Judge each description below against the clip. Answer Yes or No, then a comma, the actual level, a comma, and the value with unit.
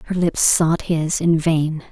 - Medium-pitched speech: Yes, medium, 165 Hz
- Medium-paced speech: Yes, average, 190 wpm